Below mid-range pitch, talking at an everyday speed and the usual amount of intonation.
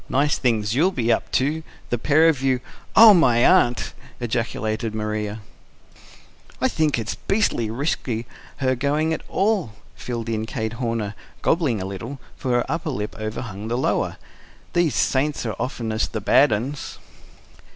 Yes: low, 120 Hz; average, 150 wpm; average, 4.8 semitones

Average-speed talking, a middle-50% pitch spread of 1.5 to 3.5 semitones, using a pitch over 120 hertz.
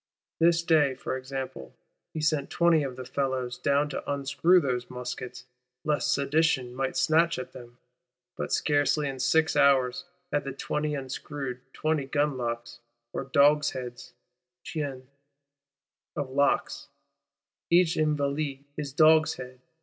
No: slow, 125 wpm; average, 2.9 semitones; medium, 140 Hz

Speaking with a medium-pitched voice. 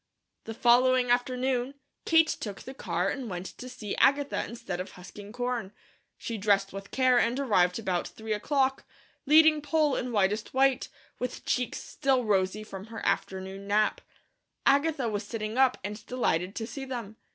No: high, 235 Hz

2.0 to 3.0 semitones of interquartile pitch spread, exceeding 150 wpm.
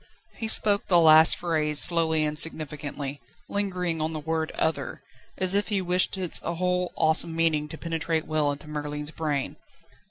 Yes: average, 2.7 semitones; average, 160 wpm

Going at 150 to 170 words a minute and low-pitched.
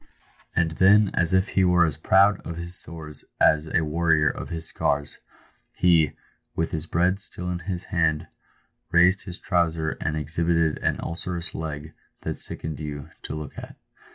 Yes: average, 165 wpm; very low, 85 Hz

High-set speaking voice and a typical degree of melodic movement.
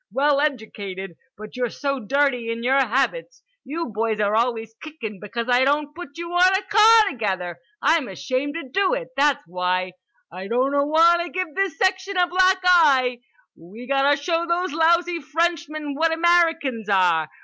No: very high, 285 Hz; wide, 6.9 semitones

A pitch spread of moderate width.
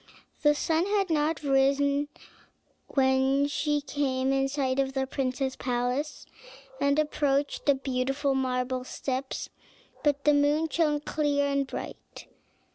No: narrow, 1.8 semitones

